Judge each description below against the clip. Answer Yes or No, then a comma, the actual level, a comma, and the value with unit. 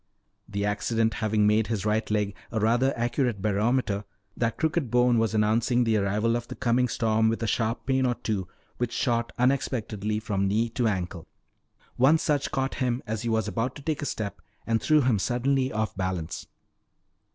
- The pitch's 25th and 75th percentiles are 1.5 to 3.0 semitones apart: Yes, average, 2.7 semitones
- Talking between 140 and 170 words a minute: No, average, 185 wpm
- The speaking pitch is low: Yes, low, 115 Hz